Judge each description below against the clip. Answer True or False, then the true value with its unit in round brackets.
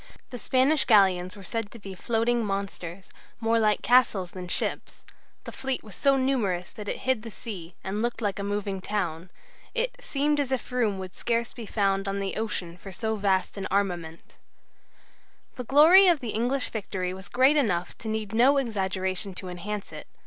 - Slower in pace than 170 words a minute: False (185 wpm)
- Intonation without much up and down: False (4.3 semitones)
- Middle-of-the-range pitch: False (210 Hz)